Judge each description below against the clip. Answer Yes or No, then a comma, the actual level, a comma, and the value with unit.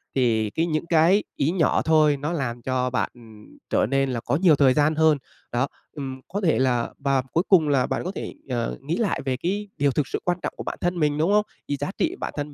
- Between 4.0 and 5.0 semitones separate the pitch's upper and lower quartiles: Yes, average, 4.3 semitones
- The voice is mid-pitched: Yes, medium, 145 Hz